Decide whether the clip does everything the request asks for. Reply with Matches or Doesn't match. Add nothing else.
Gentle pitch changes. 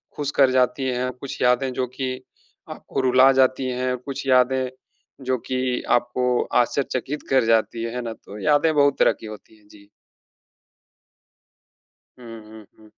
Matches